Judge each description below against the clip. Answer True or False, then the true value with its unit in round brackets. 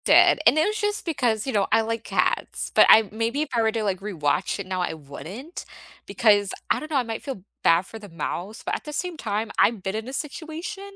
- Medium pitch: False (225 Hz)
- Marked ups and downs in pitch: True (6.9 semitones)